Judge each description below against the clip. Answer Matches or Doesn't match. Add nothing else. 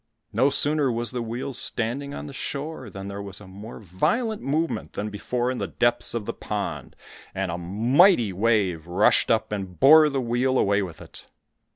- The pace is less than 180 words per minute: Doesn't match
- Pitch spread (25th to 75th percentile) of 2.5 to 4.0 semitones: Doesn't match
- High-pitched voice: Doesn't match